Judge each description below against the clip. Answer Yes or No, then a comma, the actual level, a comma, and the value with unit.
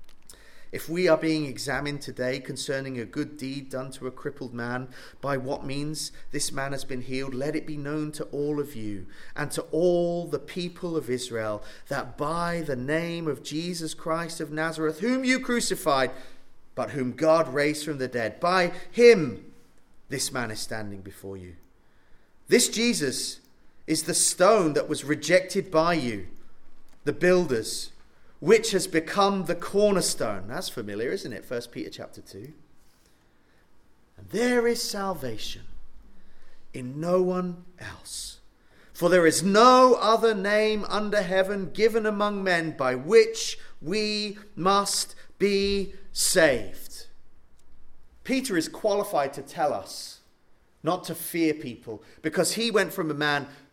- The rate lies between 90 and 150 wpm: Yes, average, 145 wpm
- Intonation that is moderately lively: No, wide, 6.4 semitones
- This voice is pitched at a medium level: Yes, medium, 160 Hz